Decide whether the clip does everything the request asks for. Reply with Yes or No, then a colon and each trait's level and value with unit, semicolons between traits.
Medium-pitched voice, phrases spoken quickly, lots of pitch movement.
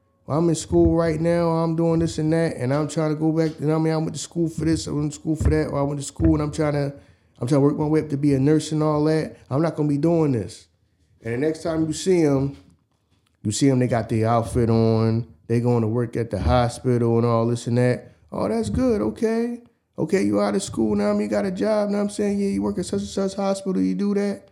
Yes: medium, 150 Hz; fast, 290 wpm; wide, 6.0 semitones